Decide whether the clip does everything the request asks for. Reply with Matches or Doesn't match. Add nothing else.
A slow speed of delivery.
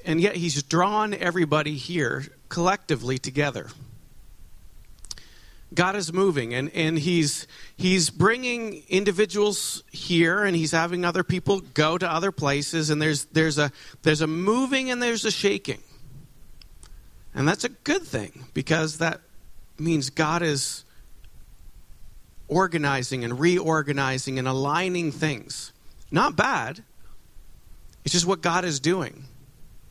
Matches